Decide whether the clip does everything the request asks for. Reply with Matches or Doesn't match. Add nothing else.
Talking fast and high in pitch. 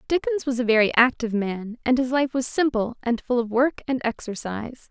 Matches